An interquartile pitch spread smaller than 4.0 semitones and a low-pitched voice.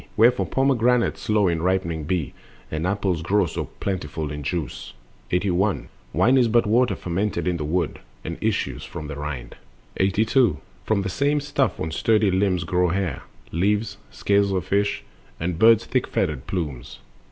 No: average, 4.6 semitones; very low, 95 Hz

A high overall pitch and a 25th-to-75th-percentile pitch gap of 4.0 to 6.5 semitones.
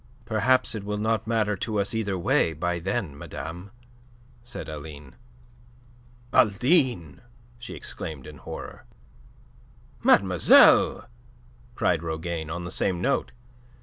No: very low, 90 Hz; wide, 5.4 semitones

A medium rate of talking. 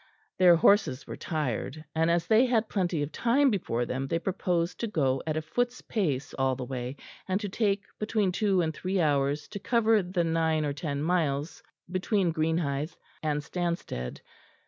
Yes: average, 175 wpm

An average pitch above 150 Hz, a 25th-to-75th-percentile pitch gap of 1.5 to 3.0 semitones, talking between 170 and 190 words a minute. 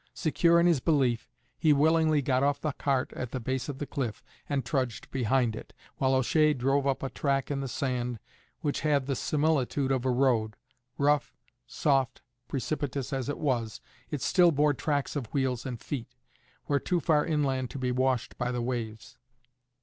No: low, 135 Hz; narrow, 2.5 semitones; average, 180 wpm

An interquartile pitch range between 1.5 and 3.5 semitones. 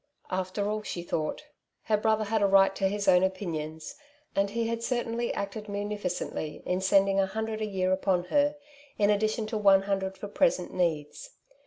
Yes: narrow, 2.5 semitones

